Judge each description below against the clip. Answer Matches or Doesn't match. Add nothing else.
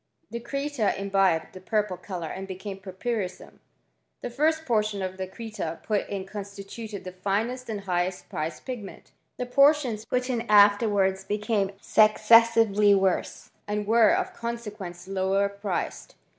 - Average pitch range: Matches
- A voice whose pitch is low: Doesn't match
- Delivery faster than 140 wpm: Doesn't match